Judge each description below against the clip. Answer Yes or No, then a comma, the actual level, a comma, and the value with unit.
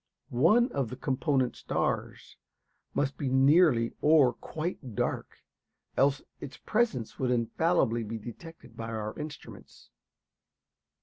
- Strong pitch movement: No, average, 4.8 semitones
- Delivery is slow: Yes, slow, 115 wpm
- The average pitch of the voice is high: No, low, 135 Hz